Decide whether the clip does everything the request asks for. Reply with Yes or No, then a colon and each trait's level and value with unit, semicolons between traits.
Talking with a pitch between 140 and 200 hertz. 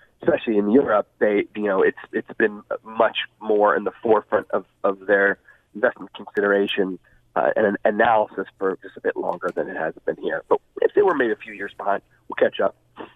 No: low, 115 Hz